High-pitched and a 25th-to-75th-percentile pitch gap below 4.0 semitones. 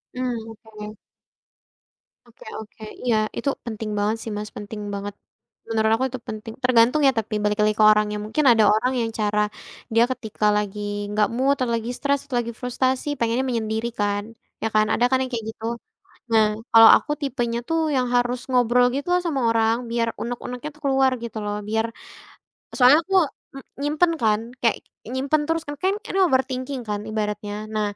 Yes: high, 230 Hz; average, 3.3 semitones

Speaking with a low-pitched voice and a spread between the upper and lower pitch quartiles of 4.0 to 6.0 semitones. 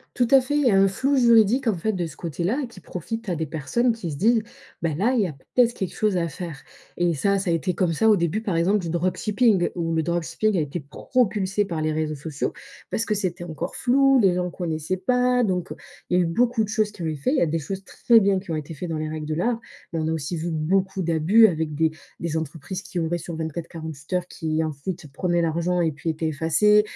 No: medium, 175 Hz; average, 4.7 semitones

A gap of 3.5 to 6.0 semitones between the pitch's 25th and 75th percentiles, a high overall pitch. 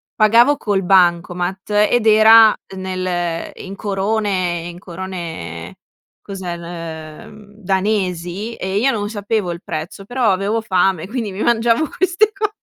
Yes: average, 3.8 semitones; high, 195 Hz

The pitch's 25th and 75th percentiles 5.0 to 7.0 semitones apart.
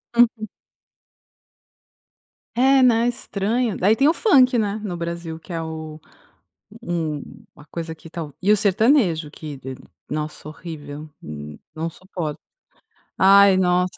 Yes: wide, 5.4 semitones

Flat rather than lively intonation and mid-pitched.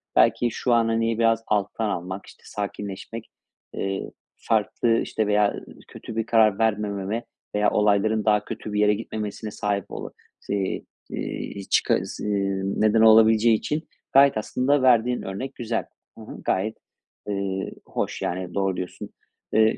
No: narrow, 2.2 semitones; low, 105 Hz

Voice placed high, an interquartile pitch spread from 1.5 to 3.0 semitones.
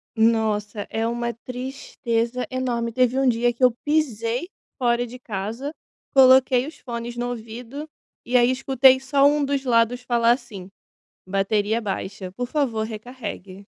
Yes: high, 240 Hz; narrow, 2.6 semitones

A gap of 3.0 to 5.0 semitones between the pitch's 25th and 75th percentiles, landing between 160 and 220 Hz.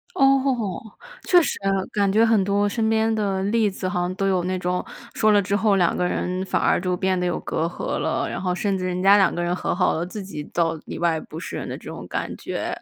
No: narrow, 2.6 semitones; high, 190 Hz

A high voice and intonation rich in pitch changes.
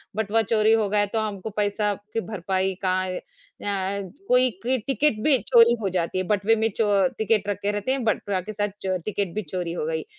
No: high, 205 Hz; average, 2.7 semitones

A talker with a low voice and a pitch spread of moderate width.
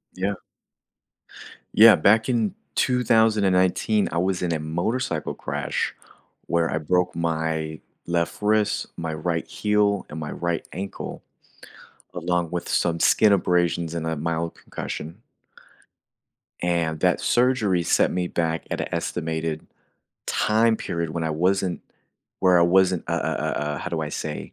Yes: very low, 85 Hz; average, 3.8 semitones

